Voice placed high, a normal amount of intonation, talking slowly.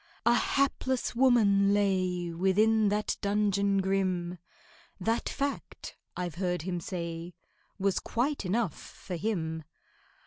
Yes: high, 195 Hz; average, 3.6 semitones; slow, 110 wpm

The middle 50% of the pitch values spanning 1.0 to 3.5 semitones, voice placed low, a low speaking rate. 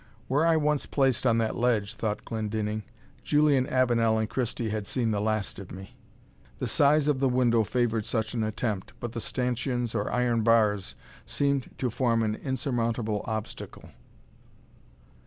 No: average, 2.9 semitones; low, 115 Hz; average, 155 wpm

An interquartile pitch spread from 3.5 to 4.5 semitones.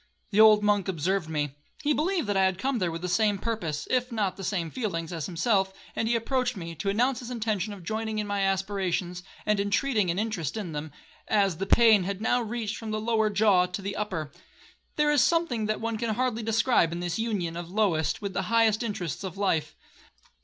Yes: average, 3.8 semitones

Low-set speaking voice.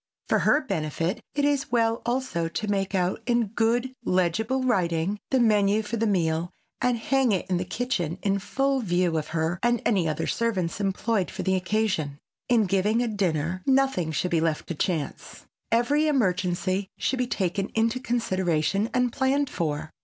No: high, 200 Hz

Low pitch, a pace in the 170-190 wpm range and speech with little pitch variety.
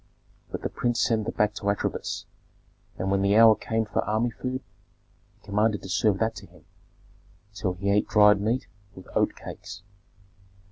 Yes: low, 105 Hz; average, 175 wpm; narrow, 2.0 semitones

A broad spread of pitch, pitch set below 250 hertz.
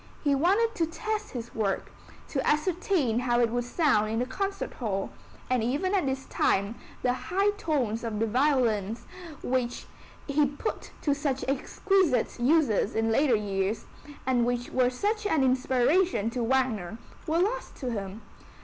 No: wide, 5.7 semitones; very high, 255 Hz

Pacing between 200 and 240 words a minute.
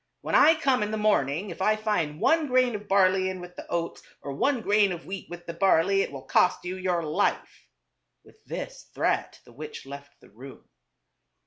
Yes: fast, 205 wpm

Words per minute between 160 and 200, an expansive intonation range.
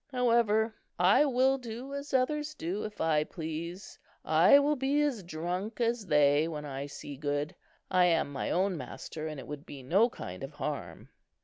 Yes: average, 180 wpm; wide, 8.4 semitones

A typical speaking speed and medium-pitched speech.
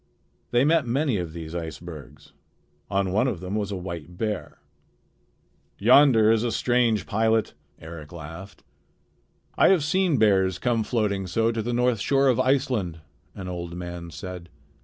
No: average, 155 wpm; low, 105 Hz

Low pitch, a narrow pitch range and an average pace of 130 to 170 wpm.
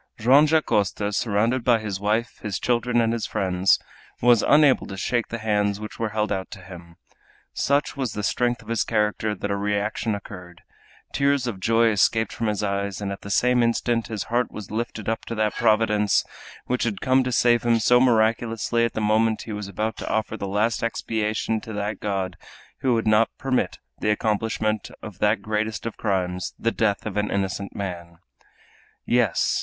No: low, 110 Hz; narrow, 2.3 semitones; average, 190 wpm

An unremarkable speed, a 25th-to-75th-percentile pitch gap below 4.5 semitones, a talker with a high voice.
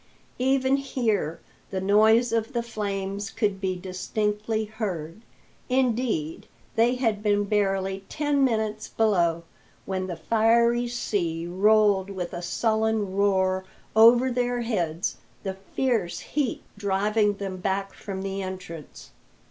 No: slow, 125 wpm; average, 3.2 semitones; high, 210 Hz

